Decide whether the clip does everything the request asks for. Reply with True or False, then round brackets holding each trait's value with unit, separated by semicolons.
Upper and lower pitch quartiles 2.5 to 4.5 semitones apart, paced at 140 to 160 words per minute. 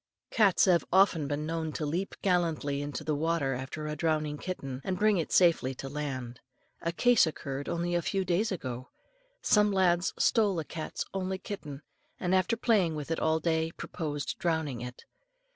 False (4.0 semitones; 175 wpm)